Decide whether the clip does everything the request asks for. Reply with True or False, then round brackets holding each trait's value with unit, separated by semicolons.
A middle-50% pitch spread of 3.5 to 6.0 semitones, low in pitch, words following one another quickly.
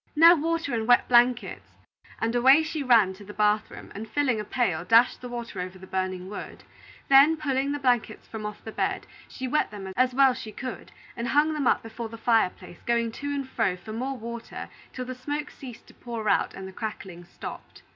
False (4.1 semitones; 235 Hz; 220 wpm)